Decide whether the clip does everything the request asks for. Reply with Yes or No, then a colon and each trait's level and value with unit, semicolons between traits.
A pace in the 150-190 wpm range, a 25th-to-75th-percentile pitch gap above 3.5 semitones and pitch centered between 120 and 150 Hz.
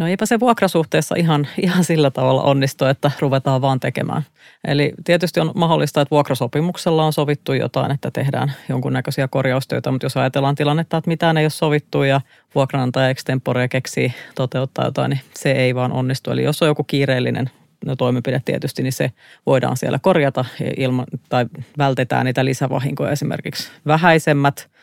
No: fast, 155 wpm; average, 2.8 semitones; medium, 140 Hz